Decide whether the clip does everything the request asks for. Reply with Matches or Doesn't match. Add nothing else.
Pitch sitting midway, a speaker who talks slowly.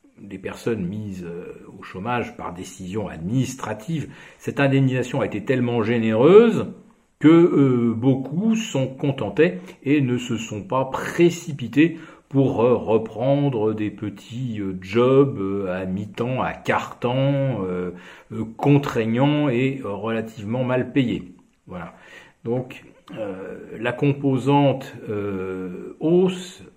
Doesn't match